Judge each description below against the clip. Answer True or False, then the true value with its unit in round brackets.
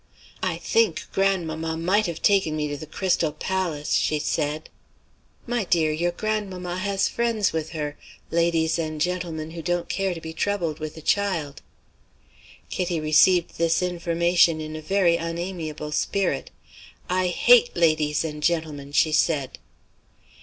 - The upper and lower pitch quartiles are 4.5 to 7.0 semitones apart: False (3.0 semitones)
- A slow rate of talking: False (145 wpm)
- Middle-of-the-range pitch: True (170 Hz)